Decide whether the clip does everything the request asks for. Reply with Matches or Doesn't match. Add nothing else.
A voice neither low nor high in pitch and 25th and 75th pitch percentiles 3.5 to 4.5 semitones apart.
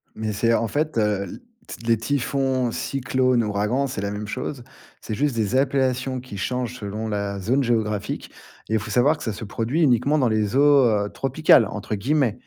Doesn't match